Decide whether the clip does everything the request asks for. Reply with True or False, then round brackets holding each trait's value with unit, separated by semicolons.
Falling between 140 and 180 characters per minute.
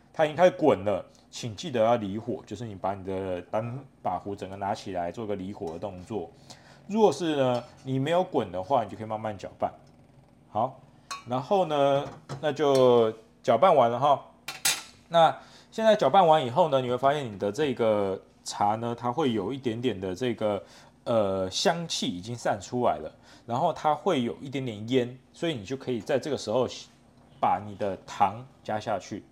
False (260 characters per minute)